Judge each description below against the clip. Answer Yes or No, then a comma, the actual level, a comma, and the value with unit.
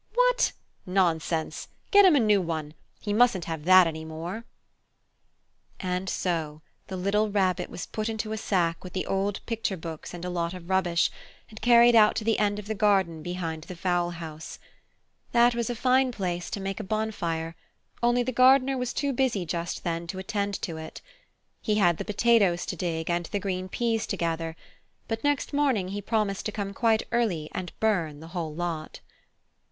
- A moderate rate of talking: Yes, average, 190 wpm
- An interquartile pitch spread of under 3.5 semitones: No, average, 4.6 semitones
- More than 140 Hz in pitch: Yes, high, 190 Hz